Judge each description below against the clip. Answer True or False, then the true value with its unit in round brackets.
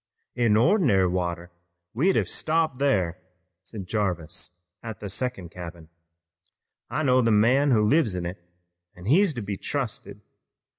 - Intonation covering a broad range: True (6.3 semitones)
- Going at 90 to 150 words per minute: True (145 wpm)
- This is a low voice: True (105 Hz)